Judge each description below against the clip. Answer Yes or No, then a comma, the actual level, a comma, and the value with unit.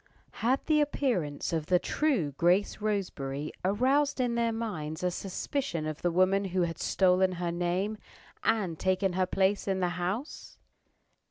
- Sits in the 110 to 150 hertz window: No, medium, 185 Hz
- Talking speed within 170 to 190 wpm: No, average, 155 wpm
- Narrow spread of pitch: No, average, 4.3 semitones